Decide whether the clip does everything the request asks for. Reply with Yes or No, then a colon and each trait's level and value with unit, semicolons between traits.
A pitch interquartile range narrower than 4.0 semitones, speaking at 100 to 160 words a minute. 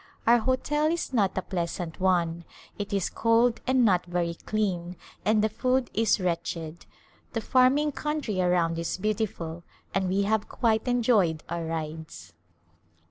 No: wide, 5.4 semitones; average, 145 wpm